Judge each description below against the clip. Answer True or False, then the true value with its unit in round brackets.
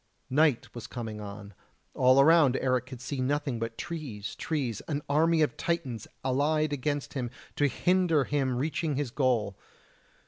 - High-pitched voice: False (135 Hz)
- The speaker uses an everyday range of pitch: True (3.9 semitones)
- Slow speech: False (150 wpm)